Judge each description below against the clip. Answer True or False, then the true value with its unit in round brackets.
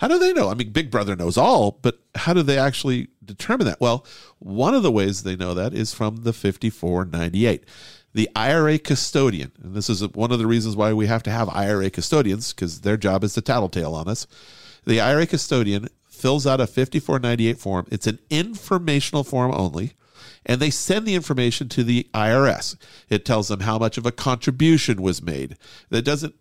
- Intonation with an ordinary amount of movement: True (4.7 semitones)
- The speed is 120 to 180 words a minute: False (200 wpm)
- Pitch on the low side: True (115 Hz)